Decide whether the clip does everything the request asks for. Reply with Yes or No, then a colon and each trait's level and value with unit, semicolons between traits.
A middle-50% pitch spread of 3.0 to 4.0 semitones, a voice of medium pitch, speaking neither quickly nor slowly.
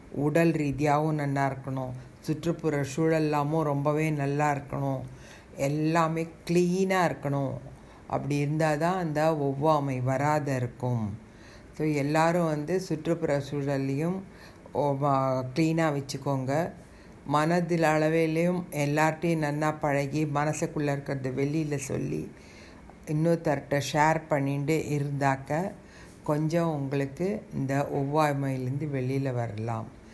No: narrow, 2.4 semitones; medium, 150 Hz; average, 90 wpm